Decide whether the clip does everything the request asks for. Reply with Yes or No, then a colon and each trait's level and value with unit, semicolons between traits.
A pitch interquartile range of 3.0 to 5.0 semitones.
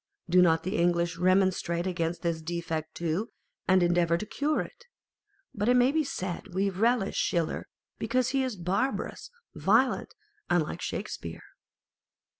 Yes: average, 3.8 semitones